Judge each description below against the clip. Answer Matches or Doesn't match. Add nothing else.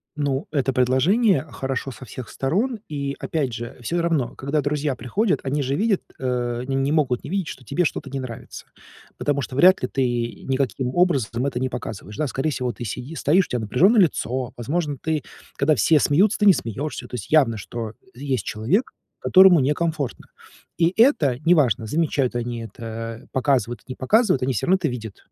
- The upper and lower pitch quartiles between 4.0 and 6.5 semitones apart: Matches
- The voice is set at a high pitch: Doesn't match